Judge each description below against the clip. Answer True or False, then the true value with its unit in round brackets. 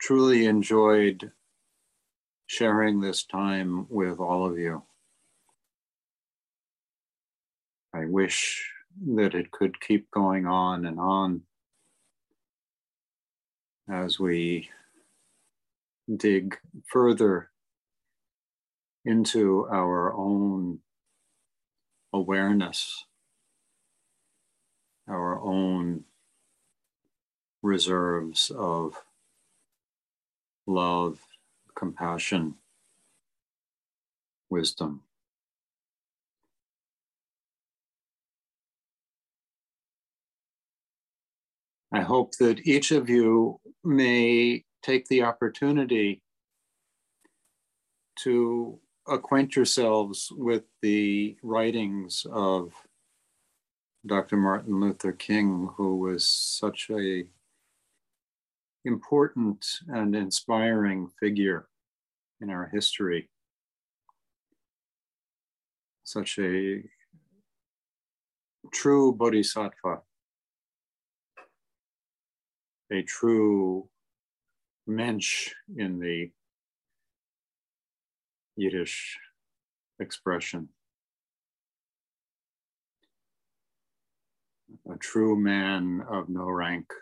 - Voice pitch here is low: True (100 Hz)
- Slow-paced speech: True (55 wpm)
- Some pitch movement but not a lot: True (3.6 semitones)